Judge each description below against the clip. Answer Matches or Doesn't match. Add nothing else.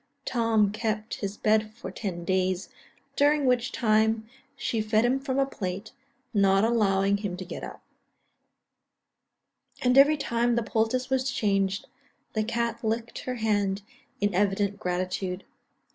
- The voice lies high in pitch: Matches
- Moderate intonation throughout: Matches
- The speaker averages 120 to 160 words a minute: Matches